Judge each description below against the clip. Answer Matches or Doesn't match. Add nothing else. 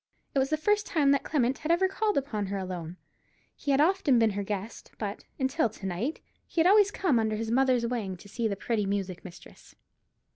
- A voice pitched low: Doesn't match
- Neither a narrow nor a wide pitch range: Doesn't match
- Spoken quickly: Matches